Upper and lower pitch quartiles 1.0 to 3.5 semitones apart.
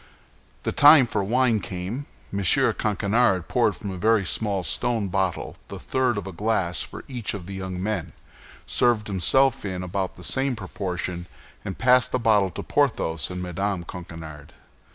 No: average, 4.3 semitones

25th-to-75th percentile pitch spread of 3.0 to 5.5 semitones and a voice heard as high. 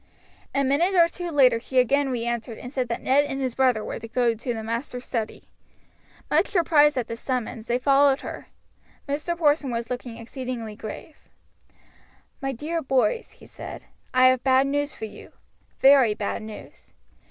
Yes: average, 3.4 semitones; very high, 255 Hz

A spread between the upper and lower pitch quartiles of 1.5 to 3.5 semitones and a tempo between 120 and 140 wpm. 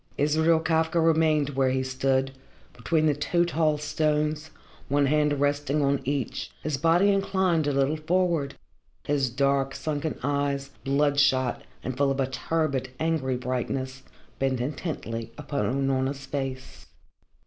Yes: narrow, 2.6 semitones; slow, 135 wpm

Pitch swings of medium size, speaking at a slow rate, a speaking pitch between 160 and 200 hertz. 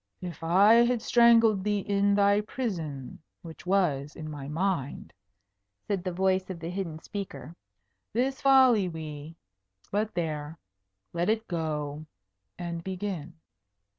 Yes: average, 4.6 semitones; slow, 130 wpm; medium, 185 Hz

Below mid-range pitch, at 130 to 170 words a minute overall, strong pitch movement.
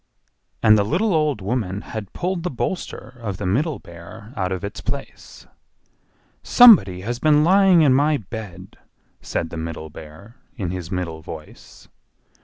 Yes: low, 110 Hz; average, 155 wpm; wide, 8.5 semitones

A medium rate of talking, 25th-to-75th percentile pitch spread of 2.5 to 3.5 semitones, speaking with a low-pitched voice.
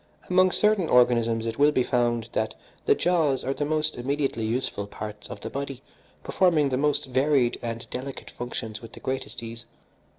No: average, 175 wpm; average, 4.0 semitones; low, 130 Hz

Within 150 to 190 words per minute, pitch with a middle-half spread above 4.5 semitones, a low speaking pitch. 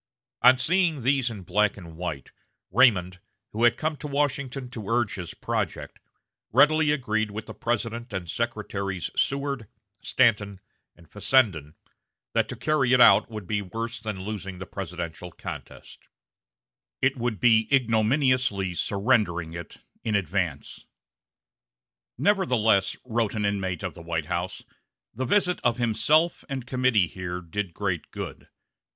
No: average, 140 wpm; average, 5.3 semitones; low, 110 Hz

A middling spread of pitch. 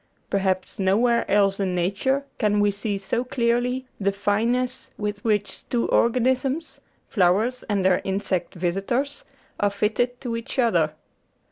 Yes: average, 3.9 semitones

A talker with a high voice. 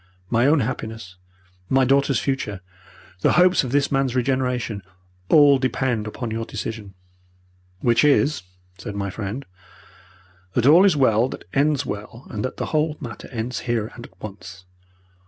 No: low, 125 Hz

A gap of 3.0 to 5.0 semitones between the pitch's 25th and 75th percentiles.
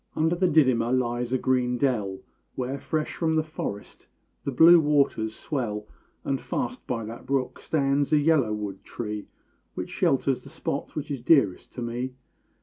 Yes: average, 4.3 semitones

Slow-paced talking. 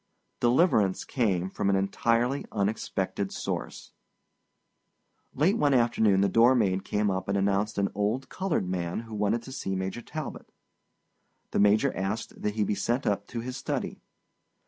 No: average, 155 wpm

